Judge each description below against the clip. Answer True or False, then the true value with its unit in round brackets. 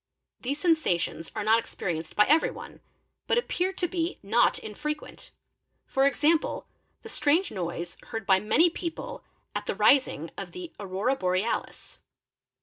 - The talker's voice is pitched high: True (270 Hz)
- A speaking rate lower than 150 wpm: True (140 wpm)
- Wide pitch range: True (8.8 semitones)